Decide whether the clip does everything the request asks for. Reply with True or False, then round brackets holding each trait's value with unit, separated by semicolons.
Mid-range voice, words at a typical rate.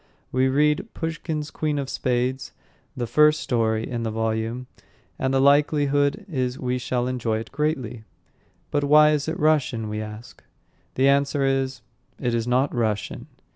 False (130 Hz; 155 wpm)